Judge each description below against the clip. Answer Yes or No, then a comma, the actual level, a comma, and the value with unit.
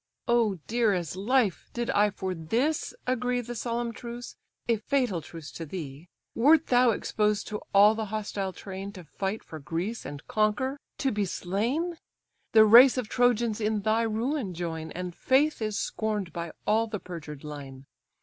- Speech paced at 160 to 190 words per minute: Yes, average, 170 wpm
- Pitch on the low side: No, high, 215 Hz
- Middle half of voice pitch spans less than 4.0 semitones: No, average, 4.7 semitones